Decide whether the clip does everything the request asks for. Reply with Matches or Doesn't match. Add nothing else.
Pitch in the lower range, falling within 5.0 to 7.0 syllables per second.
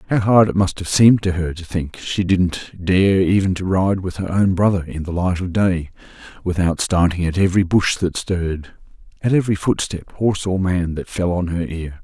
Matches